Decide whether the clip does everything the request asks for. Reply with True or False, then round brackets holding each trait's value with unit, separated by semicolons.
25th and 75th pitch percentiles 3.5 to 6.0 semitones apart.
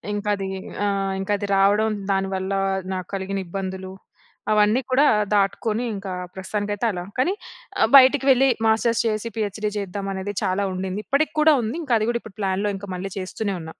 False (2.4 semitones)